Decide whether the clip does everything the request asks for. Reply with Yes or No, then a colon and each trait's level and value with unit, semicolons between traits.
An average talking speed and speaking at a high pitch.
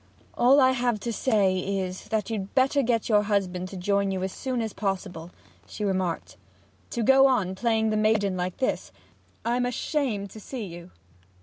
Yes: average, 180 wpm; high, 210 Hz